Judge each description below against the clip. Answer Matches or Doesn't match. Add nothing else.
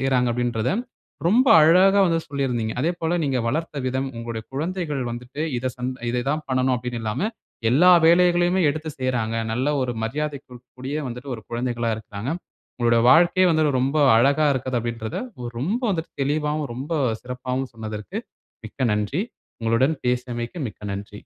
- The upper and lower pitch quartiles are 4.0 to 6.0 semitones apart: Matches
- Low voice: Matches